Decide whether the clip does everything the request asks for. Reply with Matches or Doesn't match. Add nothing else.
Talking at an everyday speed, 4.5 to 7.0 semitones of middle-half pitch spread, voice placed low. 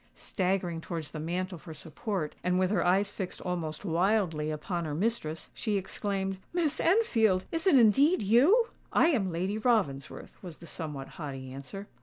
Doesn't match